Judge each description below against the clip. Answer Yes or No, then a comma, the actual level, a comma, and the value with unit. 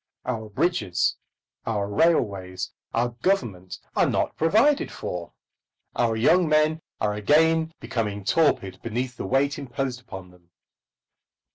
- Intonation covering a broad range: Yes, wide, 7.6 semitones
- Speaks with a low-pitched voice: Yes, low, 120 Hz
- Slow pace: Yes, slow, 120 wpm